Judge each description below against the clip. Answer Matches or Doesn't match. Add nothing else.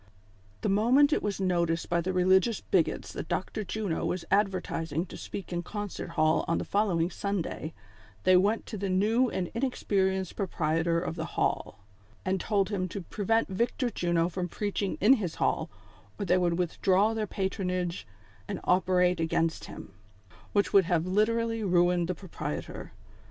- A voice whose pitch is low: Doesn't match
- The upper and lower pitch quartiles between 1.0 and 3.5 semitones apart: Matches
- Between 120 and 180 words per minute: Matches